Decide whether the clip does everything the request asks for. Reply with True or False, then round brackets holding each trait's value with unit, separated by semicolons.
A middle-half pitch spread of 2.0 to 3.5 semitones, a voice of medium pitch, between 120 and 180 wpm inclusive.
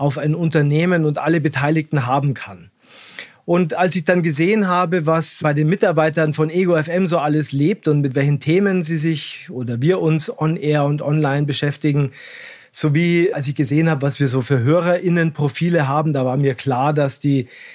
False (2.8 semitones; 155 Hz; 190 wpm)